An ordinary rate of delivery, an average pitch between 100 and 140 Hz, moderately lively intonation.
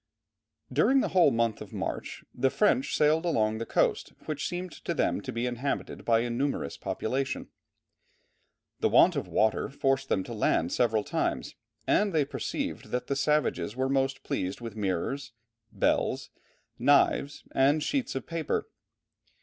Yes: average, 155 wpm; low, 135 Hz; average, 4.7 semitones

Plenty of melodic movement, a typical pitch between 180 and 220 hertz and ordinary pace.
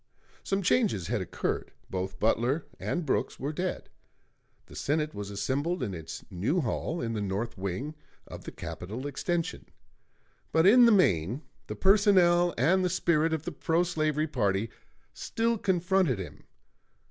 No: wide, 8.0 semitones; medium, 155 Hz; average, 150 wpm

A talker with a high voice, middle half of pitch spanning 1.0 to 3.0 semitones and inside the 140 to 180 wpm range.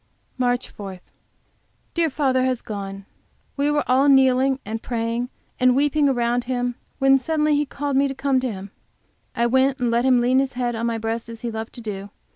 No: very high, 250 Hz; narrow, 2.6 semitones; average, 200 wpm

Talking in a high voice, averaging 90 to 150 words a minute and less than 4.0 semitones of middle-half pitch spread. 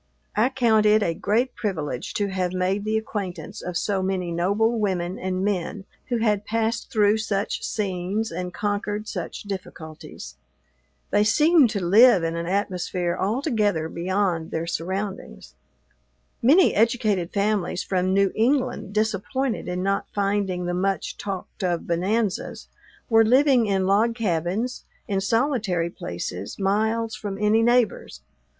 Yes: high, 200 Hz; average, 140 wpm; average, 3.4 semitones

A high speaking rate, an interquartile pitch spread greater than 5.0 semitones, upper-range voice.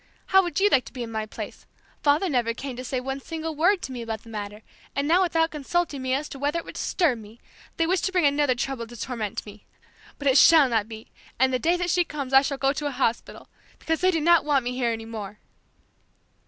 Yes: fast, 255 wpm; wide, 5.5 semitones; very high, 275 Hz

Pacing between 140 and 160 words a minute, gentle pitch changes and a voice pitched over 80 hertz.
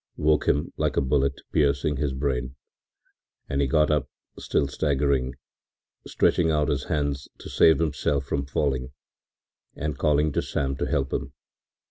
No: average, 155 wpm; narrow, 1.7 semitones; very low, 70 Hz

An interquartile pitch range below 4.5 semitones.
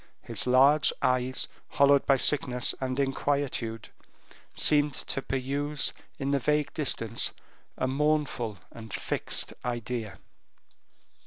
Yes: narrow, 2.5 semitones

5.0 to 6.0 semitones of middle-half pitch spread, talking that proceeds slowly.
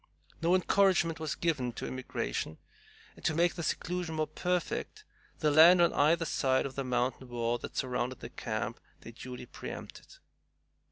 No: wide, 5.4 semitones; average, 160 wpm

